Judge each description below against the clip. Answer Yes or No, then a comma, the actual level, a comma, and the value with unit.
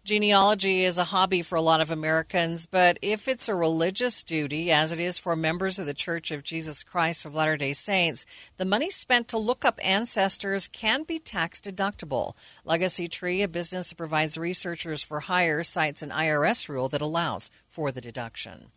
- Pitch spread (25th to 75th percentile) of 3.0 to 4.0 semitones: Yes, average, 3.6 semitones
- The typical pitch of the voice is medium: Yes, medium, 170 Hz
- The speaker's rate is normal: Yes, average, 190 wpm